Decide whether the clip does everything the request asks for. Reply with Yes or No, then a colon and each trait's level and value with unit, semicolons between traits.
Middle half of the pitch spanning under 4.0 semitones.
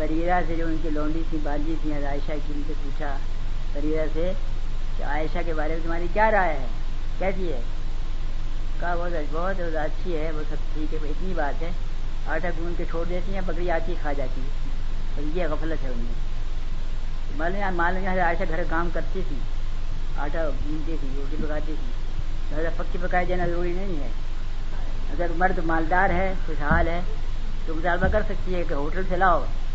No: average, 4.3 semitones